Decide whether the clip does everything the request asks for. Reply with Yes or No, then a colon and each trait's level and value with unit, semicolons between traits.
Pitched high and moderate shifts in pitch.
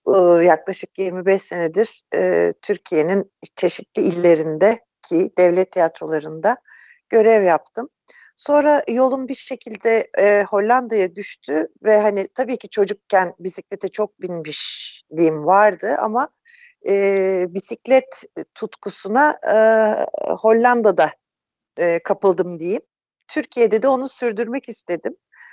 Yes: high, 205 Hz; average, 4.6 semitones